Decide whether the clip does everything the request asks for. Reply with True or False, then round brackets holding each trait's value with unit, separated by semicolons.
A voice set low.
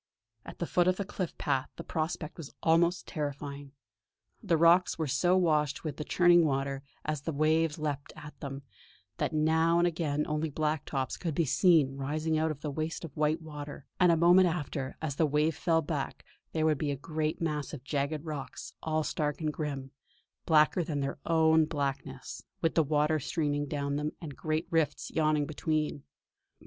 False (155 Hz)